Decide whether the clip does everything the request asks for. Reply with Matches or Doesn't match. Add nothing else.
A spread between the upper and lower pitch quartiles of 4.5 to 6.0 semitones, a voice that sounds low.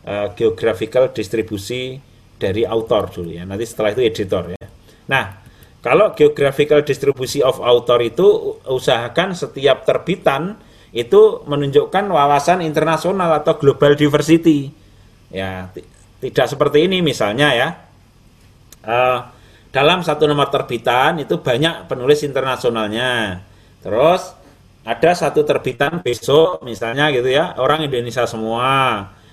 Matches